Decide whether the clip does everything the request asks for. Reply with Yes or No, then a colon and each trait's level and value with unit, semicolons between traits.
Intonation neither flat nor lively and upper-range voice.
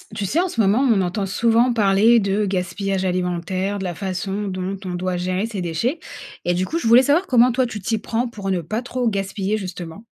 Yes: average, 3.8 semitones; high, 200 Hz